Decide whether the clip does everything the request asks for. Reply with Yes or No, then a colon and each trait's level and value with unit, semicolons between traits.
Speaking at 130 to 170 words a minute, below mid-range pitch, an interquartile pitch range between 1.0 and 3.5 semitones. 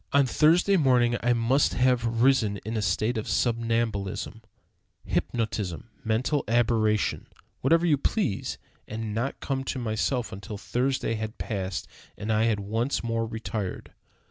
Yes: average, 140 wpm; low, 115 Hz; average, 2.9 semitones